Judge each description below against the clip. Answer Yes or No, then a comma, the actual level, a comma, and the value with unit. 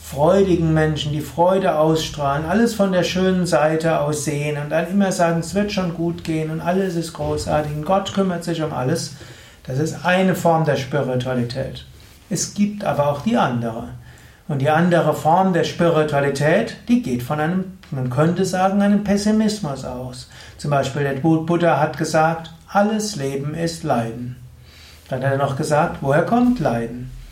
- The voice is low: No, medium, 160 Hz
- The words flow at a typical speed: Yes, average, 165 wpm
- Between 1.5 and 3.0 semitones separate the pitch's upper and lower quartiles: No, average, 4.0 semitones